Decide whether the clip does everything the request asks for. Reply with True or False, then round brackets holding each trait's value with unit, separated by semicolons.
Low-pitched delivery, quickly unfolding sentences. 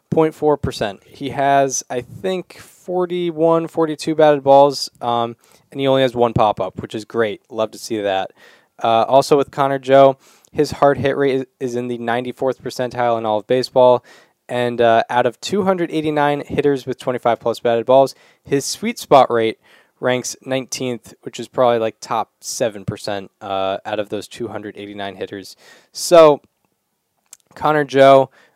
False (130 Hz; 150 wpm)